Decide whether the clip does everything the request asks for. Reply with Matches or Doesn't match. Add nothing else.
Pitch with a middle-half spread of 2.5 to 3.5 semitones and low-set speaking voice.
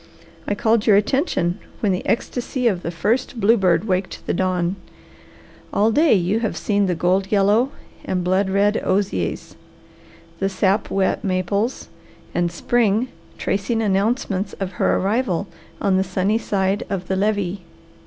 Doesn't match